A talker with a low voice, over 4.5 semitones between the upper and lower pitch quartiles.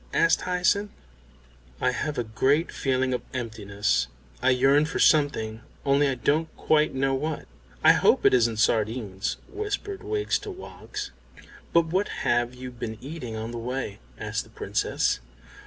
Yes: low, 130 Hz; wide, 5.4 semitones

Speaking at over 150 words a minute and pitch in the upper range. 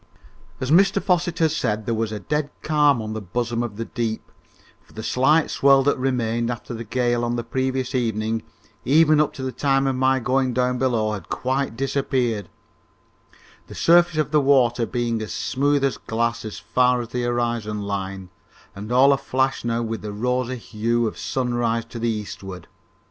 No: average, 185 wpm; low, 120 Hz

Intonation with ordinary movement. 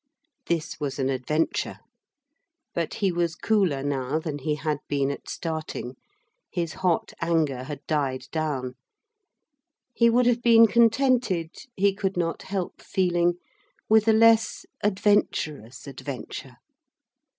No: wide, 6.1 semitones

